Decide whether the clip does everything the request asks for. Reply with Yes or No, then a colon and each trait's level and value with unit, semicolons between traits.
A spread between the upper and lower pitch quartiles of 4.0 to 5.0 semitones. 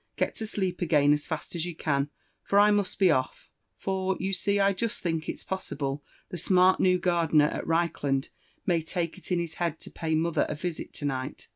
No: average, 3.6 semitones